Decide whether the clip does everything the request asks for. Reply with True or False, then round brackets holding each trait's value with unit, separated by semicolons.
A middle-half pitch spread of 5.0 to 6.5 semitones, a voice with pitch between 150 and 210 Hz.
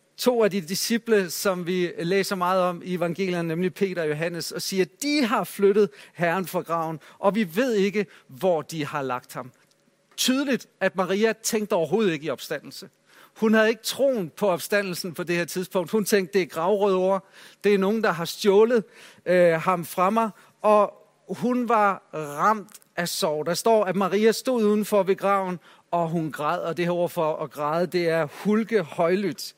False (3.5 semitones; 190 Hz)